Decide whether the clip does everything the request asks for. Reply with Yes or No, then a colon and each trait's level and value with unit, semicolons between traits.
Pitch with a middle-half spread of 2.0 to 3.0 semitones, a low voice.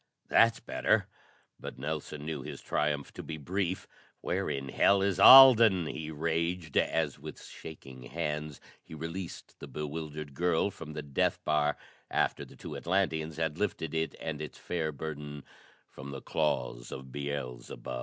Yes: narrow, 2.4 semitones; very low, 75 Hz